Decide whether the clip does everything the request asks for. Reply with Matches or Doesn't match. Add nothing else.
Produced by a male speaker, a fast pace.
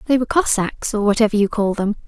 Doesn't match